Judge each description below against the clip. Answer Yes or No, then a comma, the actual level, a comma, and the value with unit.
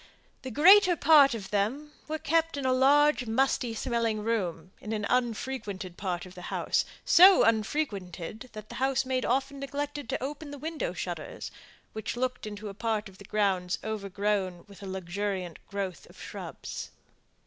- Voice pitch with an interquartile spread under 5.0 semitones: No, wide, 5.6 semitones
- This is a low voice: No, high, 225 Hz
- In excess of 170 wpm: No, average, 165 wpm